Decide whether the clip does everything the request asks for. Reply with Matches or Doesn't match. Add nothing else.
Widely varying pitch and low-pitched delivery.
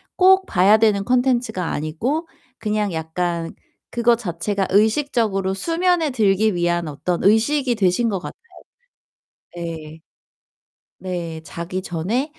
Doesn't match